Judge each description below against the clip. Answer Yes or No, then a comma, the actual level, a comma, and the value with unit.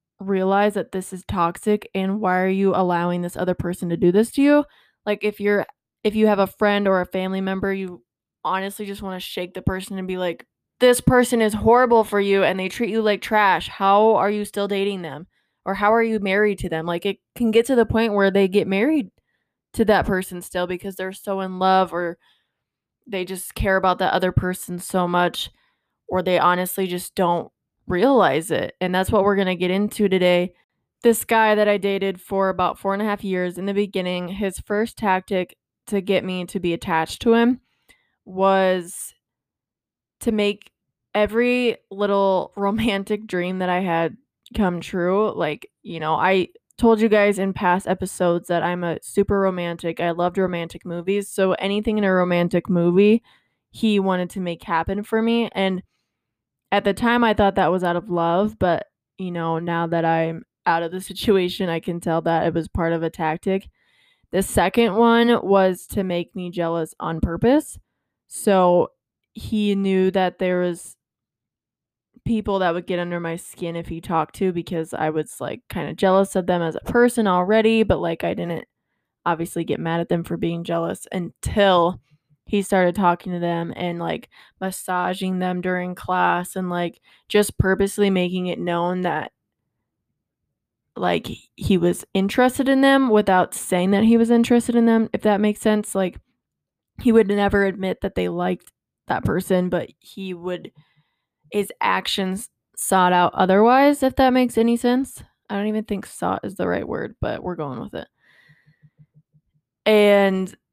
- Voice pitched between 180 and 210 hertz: Yes, high, 190 Hz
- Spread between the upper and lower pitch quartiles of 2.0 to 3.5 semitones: Yes, average, 2.7 semitones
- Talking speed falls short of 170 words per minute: No, average, 185 wpm